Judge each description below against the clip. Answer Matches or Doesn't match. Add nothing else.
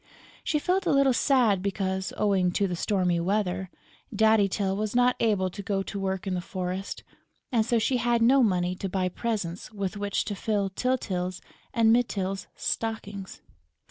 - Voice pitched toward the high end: Matches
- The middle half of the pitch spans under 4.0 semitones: Matches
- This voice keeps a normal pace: Matches